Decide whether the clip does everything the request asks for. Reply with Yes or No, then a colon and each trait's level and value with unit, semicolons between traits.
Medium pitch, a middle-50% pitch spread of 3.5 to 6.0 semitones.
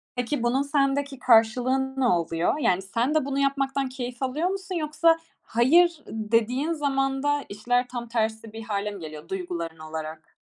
No: very high, 250 Hz; average, 4.6 semitones